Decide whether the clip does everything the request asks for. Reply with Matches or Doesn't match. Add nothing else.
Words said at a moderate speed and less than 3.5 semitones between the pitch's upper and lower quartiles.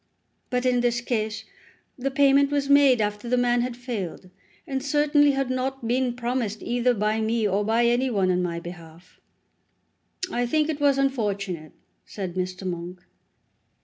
Doesn't match